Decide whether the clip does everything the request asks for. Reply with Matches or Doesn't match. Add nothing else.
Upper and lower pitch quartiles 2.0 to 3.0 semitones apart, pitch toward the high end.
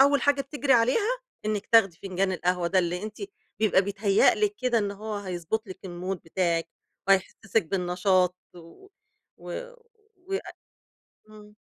Doesn't match